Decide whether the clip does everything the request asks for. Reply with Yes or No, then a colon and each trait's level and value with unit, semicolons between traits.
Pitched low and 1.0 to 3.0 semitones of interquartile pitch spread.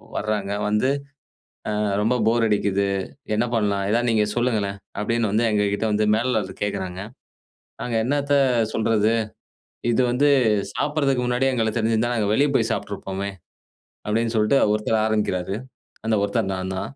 Yes: low, 110 Hz; average, 2.7 semitones